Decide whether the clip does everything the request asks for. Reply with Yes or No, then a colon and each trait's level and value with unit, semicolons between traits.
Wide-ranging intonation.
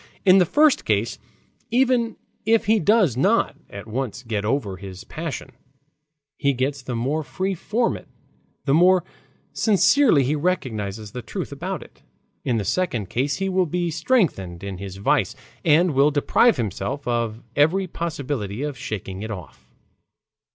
Yes: wide, 8.6 semitones